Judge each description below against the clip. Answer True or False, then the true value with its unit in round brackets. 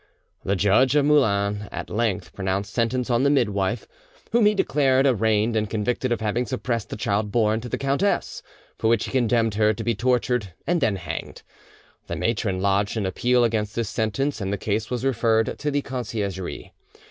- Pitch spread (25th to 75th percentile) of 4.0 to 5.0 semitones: False (3.5 semitones)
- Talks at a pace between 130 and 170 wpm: False (185 wpm)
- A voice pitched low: True (115 Hz)